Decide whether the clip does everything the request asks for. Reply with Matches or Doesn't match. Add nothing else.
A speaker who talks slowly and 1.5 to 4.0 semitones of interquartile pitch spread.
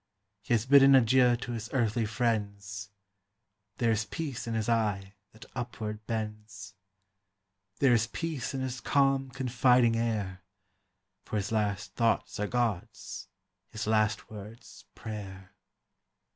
Matches